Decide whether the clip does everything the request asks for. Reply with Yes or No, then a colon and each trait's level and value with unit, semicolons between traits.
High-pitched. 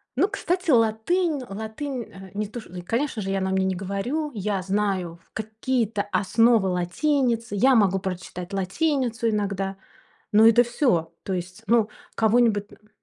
Yes: high, 215 Hz